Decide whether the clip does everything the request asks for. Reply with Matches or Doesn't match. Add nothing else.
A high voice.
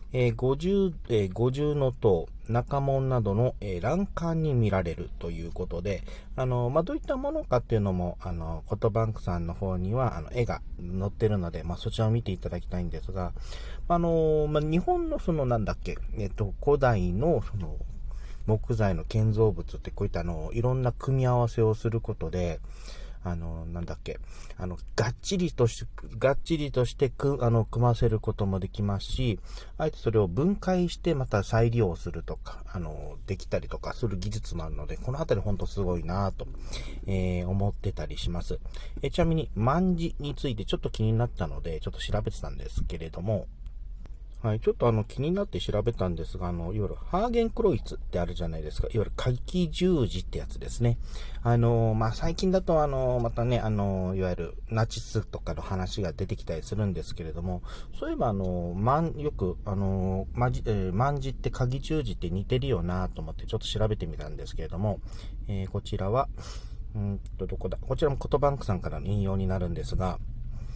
Doesn't match